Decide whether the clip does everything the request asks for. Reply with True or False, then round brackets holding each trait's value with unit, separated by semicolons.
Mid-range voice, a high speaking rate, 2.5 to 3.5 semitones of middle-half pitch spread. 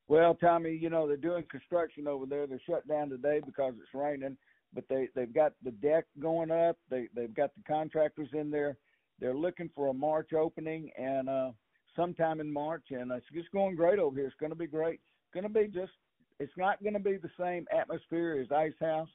True (155 Hz; 220 wpm; 3.2 semitones)